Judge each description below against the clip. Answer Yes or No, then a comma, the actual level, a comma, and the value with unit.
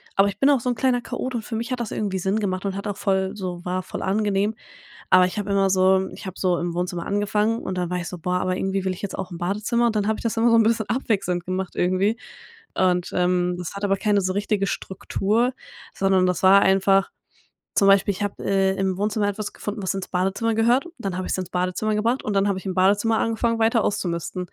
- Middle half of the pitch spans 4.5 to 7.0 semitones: No, narrow, 2.6 semitones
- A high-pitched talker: Yes, high, 195 Hz